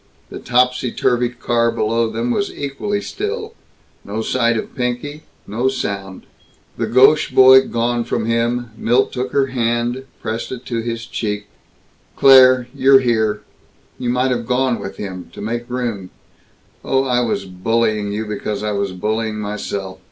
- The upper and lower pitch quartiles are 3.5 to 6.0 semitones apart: No, average, 2.9 semitones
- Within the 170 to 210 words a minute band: No, average, 155 wpm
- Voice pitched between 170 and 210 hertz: No, low, 120 Hz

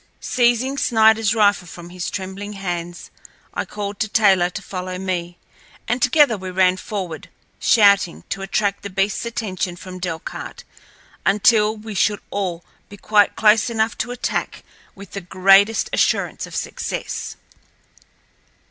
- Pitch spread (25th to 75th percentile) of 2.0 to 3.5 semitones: Yes, average, 3.0 semitones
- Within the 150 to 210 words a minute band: No, average, 140 wpm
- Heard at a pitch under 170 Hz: No, high, 200 Hz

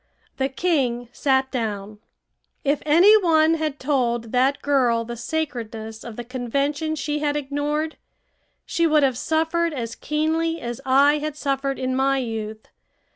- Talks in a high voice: Yes, very high, 275 Hz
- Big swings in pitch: No, average, 4.2 semitones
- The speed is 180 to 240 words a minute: No, average, 145 wpm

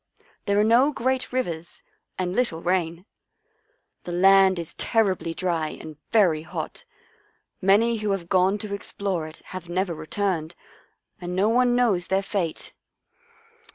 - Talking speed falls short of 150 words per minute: Yes, average, 140 wpm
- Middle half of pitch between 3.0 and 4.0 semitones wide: Yes, average, 3.5 semitones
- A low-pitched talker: No, high, 190 Hz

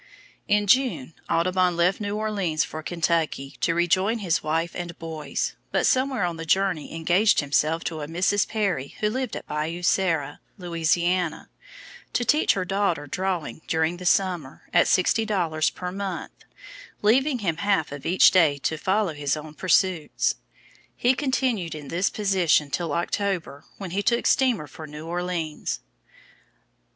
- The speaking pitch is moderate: Yes, medium, 175 Hz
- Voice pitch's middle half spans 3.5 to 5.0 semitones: Yes, average, 3.9 semitones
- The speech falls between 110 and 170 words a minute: Yes, average, 155 wpm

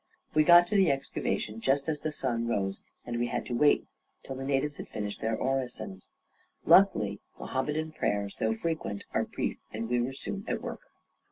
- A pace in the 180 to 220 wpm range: Yes, average, 185 wpm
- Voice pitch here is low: Yes, low, 130 Hz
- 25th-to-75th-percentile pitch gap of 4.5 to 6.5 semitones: Yes, average, 5.0 semitones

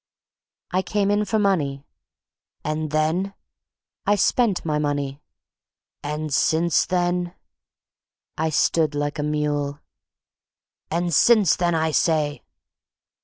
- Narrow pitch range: No, average, 3.4 semitones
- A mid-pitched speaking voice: Yes, medium, 160 Hz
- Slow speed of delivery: Yes, slow, 110 wpm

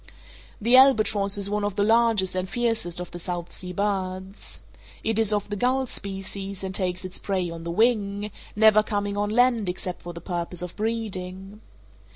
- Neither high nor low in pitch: No, high, 200 Hz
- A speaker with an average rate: Yes, average, 185 wpm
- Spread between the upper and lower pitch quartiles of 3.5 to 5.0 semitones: No, average, 2.9 semitones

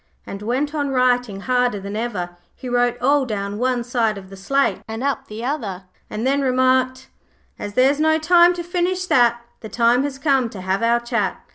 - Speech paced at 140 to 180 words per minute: No, fast, 205 wpm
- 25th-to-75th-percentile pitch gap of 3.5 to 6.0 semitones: Yes, average, 4.0 semitones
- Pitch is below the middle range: No, high, 245 Hz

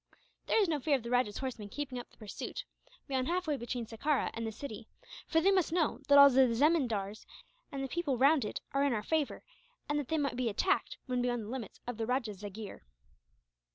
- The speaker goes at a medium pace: No, fast, 215 wpm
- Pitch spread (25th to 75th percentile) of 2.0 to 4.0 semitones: No, average, 4.4 semitones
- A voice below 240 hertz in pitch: No, very high, 260 Hz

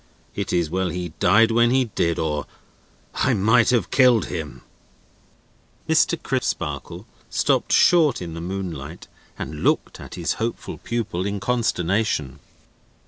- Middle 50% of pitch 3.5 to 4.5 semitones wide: No, wide, 5.4 semitones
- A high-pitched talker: No, very low, 95 Hz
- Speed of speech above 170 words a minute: No, slow, 135 wpm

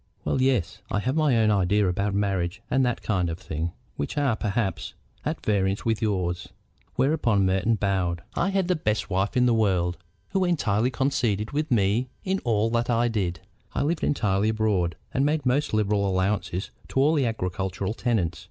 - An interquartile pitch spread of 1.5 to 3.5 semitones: No, average, 4.8 semitones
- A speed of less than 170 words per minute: No, average, 180 wpm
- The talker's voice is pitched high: No, low, 105 Hz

